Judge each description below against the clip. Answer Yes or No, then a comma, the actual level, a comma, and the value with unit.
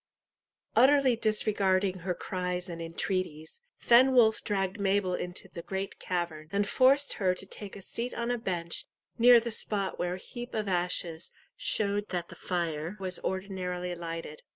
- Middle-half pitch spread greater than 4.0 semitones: No, average, 3.2 semitones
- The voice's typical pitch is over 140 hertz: Yes, high, 190 Hz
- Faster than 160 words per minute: No, average, 155 wpm